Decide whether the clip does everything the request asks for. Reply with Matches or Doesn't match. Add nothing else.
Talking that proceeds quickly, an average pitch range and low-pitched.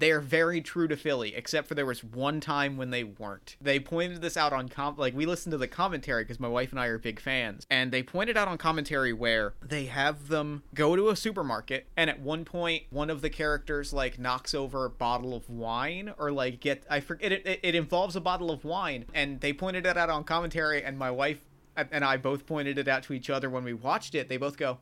Doesn't match